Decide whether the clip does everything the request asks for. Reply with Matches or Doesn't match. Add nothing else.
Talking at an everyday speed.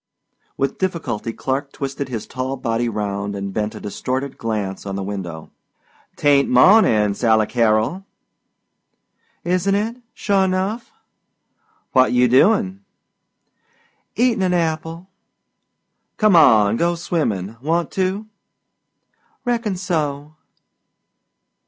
Doesn't match